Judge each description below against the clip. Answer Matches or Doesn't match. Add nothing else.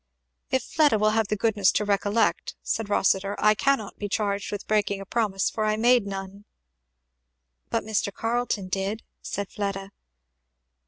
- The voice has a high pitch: Matches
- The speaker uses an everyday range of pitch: Doesn't match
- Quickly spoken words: Doesn't match